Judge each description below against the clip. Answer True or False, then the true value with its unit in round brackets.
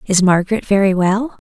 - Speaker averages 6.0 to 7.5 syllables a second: False (5.3 syllables/s)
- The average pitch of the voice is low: False (195 Hz)